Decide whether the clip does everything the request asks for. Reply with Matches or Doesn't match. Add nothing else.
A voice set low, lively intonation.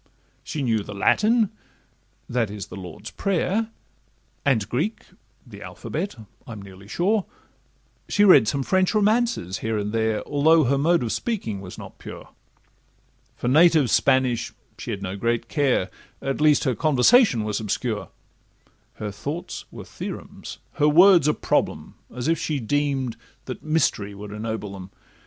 Matches